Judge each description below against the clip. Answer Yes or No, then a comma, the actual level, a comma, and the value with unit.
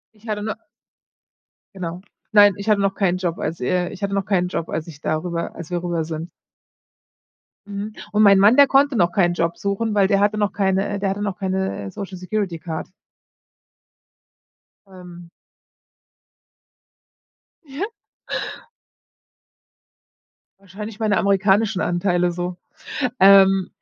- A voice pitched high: Yes, high, 195 Hz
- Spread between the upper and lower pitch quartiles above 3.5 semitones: No, narrow, 2.6 semitones